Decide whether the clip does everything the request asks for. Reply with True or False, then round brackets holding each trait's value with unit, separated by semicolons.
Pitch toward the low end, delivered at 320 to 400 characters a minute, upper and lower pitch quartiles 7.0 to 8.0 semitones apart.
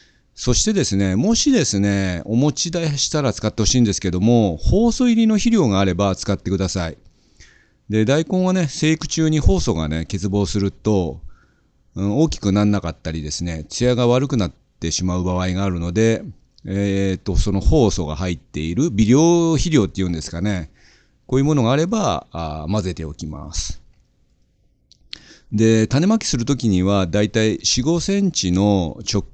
True (105 Hz; 335 characters per minute; 7.3 semitones)